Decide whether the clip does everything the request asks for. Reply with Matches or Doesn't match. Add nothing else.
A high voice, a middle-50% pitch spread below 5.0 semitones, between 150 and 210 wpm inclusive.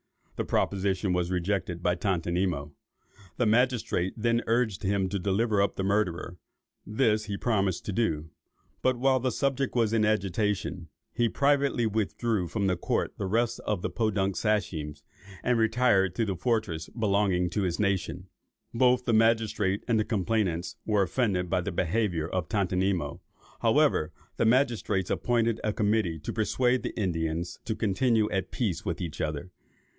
Doesn't match